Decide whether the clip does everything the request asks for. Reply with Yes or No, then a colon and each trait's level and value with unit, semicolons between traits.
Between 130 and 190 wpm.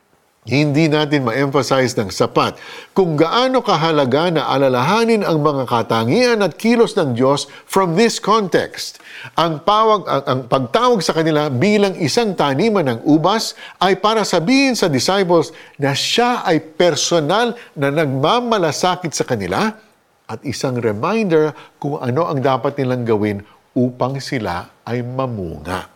Yes: average, 135 wpm